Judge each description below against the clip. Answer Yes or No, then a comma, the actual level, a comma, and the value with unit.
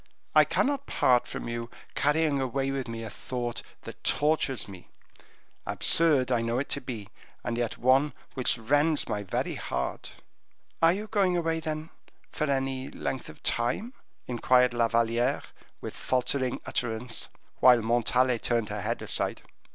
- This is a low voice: Yes, low, 130 Hz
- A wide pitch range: No, average, 3.8 semitones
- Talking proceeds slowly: No, average, 150 wpm